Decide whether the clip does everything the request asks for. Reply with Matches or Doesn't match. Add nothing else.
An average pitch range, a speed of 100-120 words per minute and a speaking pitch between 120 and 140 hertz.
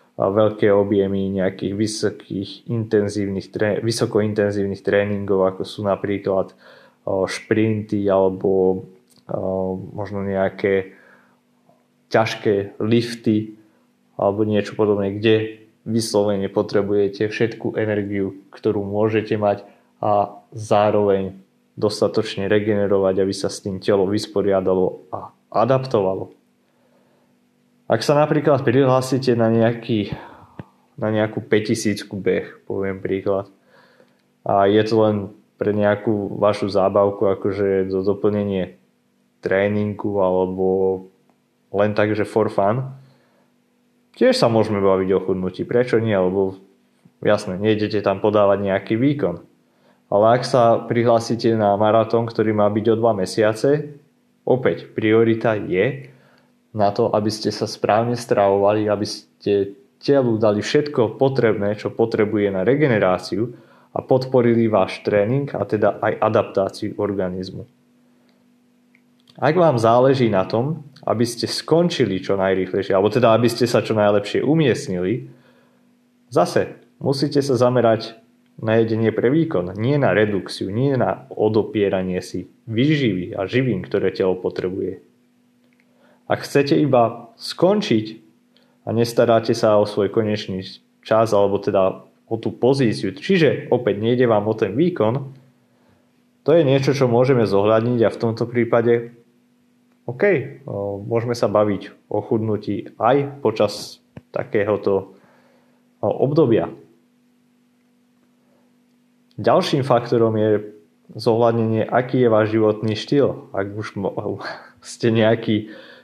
Doesn't match